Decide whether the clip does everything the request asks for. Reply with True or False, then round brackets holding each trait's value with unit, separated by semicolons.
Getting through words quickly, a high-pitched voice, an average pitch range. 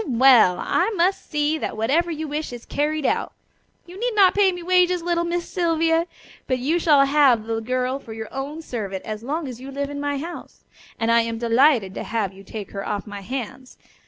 False (215 wpm; 275 Hz; 6.3 semitones)